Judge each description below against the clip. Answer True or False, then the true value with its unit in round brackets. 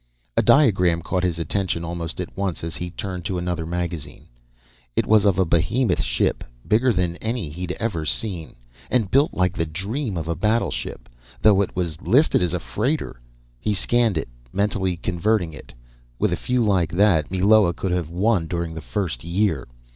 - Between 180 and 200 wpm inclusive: True (185 wpm)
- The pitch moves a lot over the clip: False (4.0 semitones)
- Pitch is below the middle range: True (90 Hz)